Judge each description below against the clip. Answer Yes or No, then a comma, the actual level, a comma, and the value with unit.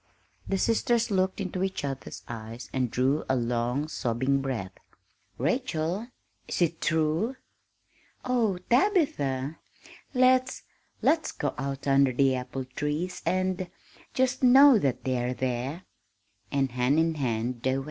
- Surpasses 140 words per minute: No, slow, 135 wpm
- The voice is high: No, medium, 145 Hz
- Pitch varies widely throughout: Yes, wide, 6.8 semitones